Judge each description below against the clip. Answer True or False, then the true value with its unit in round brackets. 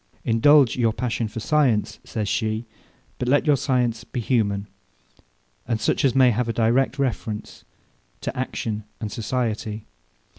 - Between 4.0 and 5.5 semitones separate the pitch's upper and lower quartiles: False (2.8 semitones)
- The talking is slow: False (145 wpm)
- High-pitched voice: False (115 Hz)